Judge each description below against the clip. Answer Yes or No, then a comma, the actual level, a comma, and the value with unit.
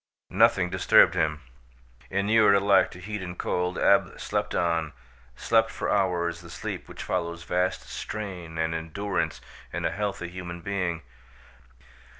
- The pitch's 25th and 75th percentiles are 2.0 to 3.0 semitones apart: Yes, average, 2.7 semitones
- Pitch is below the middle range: Yes, very low, 90 Hz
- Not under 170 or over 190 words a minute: No, average, 140 wpm